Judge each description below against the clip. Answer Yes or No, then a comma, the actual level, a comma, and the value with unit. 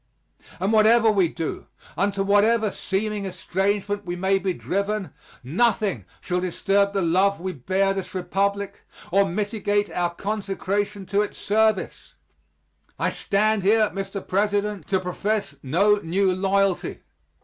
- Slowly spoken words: Yes, slow, 130 wpm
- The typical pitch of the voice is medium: No, high, 200 Hz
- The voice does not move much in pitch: Yes, narrow, 1.7 semitones